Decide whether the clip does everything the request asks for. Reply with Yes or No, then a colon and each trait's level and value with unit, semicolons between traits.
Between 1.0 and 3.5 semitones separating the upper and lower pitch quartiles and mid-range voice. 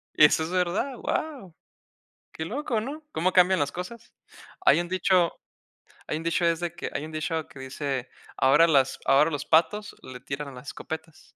No: average, 4.0 semitones; medium, 165 Hz